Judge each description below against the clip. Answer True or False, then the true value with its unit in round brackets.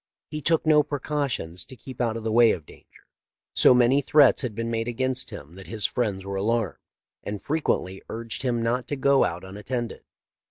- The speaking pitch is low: True (120 Hz)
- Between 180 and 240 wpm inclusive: True (195 wpm)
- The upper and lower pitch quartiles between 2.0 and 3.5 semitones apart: False (4.2 semitones)